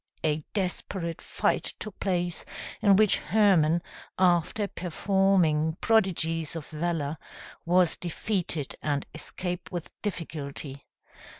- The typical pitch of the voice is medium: Yes, medium, 175 Hz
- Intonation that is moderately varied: Yes, average, 3.5 semitones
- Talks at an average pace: No, slow, 100 wpm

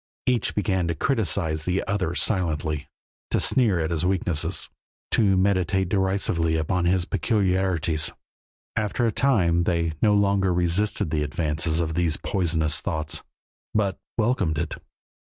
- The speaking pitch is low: Yes, very low, 90 Hz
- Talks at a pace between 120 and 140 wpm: Yes, slow, 135 wpm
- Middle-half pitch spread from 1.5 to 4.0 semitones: Yes, average, 3.6 semitones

